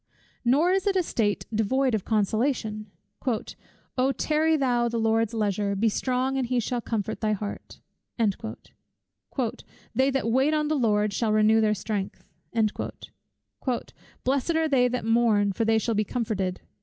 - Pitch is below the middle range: No, high, 230 Hz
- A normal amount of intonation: Yes, average, 3.7 semitones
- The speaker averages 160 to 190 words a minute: No, average, 150 wpm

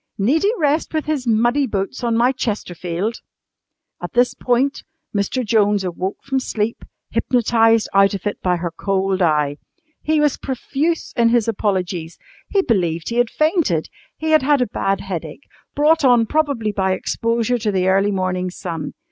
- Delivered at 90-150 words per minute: No, average, 165 wpm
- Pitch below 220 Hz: No, high, 225 Hz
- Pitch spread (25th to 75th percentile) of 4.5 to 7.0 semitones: Yes, wide, 5.5 semitones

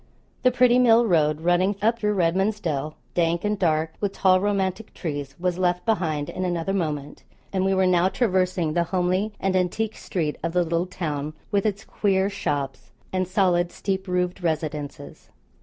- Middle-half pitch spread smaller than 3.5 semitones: Yes, average, 3.0 semitones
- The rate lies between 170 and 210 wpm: Yes, average, 175 wpm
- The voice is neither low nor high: Yes, medium, 180 Hz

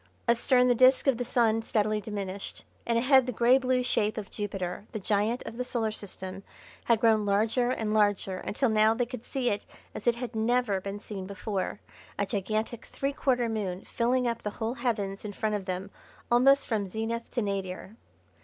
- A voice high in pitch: Yes, high, 220 Hz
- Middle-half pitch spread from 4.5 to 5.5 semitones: No, average, 3.1 semitones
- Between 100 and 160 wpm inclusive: No, average, 190 wpm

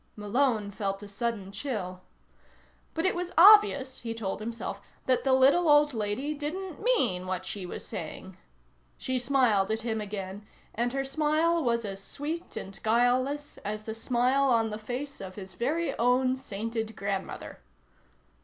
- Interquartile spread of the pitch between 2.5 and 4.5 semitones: No, average, 5.3 semitones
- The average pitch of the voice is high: Yes, high, 240 Hz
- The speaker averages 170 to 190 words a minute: No, average, 155 wpm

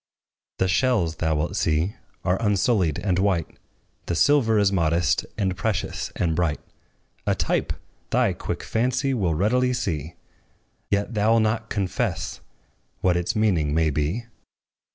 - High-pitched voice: No, very low, 95 Hz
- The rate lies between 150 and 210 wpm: No, average, 140 wpm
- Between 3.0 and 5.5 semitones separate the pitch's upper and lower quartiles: Yes, average, 4.8 semitones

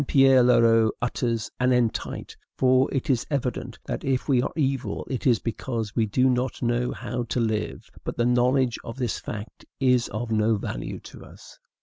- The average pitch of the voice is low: Yes, low, 120 Hz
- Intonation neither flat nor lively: No, narrow, 2.2 semitones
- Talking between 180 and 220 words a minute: Yes, average, 185 wpm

